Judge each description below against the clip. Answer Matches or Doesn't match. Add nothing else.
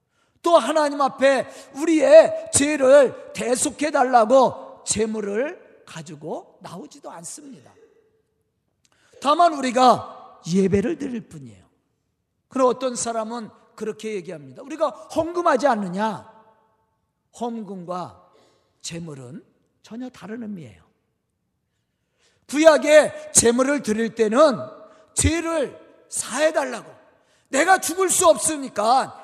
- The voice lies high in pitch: Matches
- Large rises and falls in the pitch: Matches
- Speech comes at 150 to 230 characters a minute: Matches